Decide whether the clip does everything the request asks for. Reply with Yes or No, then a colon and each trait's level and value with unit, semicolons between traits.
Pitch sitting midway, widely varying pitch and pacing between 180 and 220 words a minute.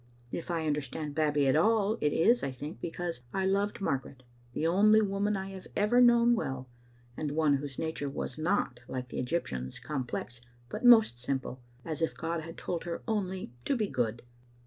Yes: medium, 160 Hz; wide, 6.6 semitones; average, 185 wpm